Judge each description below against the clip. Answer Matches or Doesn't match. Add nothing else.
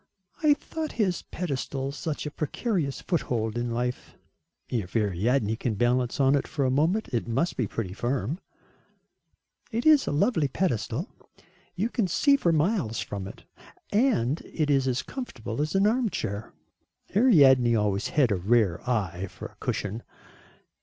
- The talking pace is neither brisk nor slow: Matches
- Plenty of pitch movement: Matches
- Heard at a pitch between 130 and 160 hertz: Matches